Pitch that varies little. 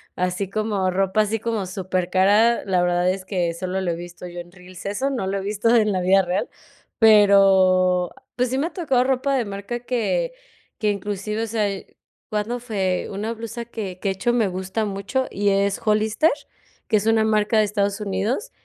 No: average, 3.1 semitones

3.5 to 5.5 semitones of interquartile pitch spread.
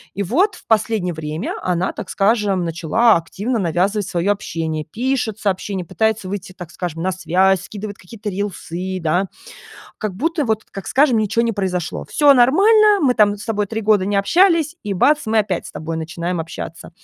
Yes: average, 4.0 semitones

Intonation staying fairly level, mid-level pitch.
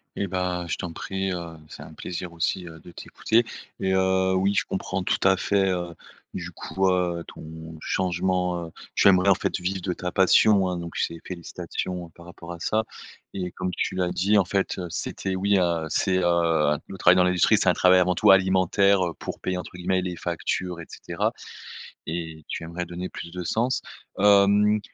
No: narrow, 1.7 semitones; very low, 90 Hz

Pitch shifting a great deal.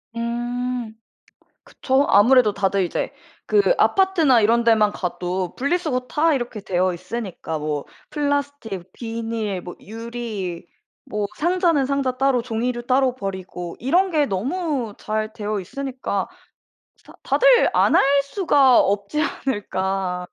Yes: wide, 5.7 semitones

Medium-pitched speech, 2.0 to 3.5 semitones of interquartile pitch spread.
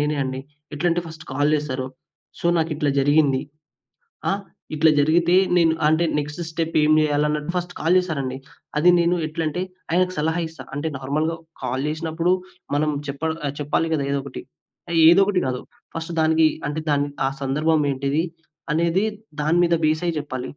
Yes: medium, 155 Hz; narrow, 2.4 semitones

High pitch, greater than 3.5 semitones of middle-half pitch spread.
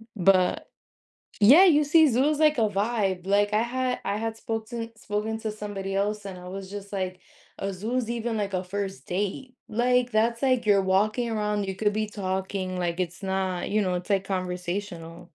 No: high, 205 Hz; average, 3.1 semitones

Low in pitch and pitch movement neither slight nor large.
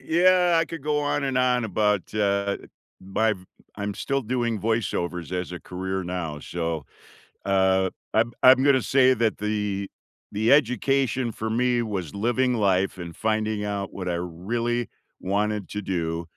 Yes: low, 105 Hz; average, 4.5 semitones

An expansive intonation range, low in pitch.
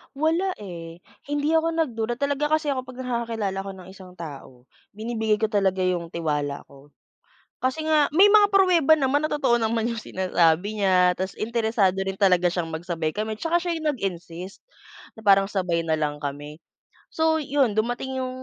No: wide, 7.9 semitones; high, 215 Hz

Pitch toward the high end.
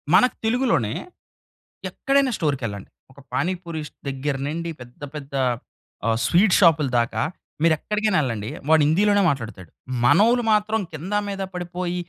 No: medium, 165 Hz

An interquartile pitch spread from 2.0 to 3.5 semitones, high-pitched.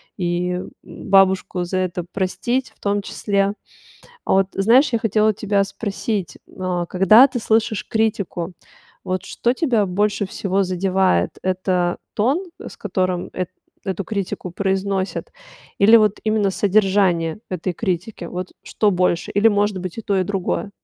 Yes: narrow, 2.6 semitones; high, 195 Hz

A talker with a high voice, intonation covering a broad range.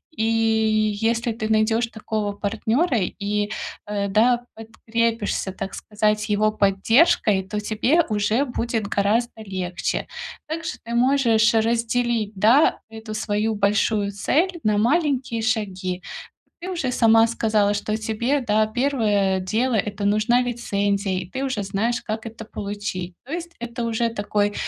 No: high, 220 Hz; narrow, 2.5 semitones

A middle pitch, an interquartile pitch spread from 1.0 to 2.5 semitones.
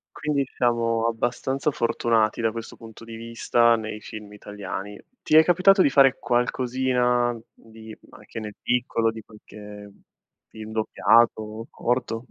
No: low, 115 Hz; narrow, 2.0 semitones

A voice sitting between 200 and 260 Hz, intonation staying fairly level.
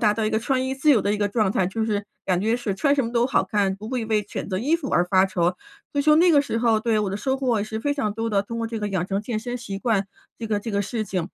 No: high, 220 Hz; average, 3.3 semitones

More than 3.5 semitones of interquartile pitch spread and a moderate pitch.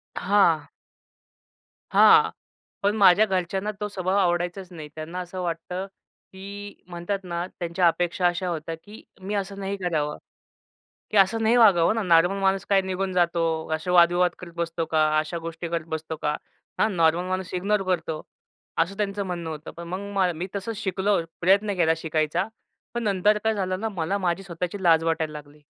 No: average, 2.8 semitones; medium, 180 Hz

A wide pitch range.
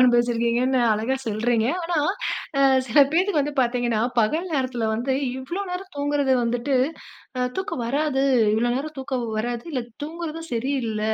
No: average, 3.8 semitones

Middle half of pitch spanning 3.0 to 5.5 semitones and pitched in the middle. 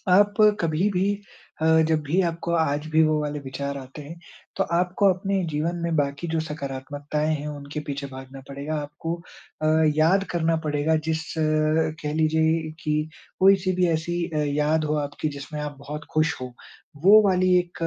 No: narrow, 2.4 semitones; medium, 155 Hz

